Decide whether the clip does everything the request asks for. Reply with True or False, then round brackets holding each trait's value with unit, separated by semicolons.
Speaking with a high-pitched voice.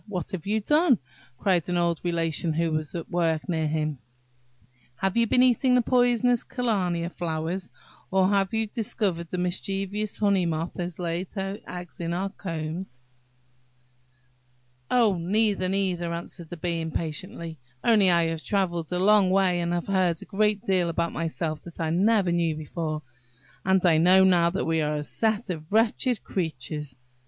False (180 Hz)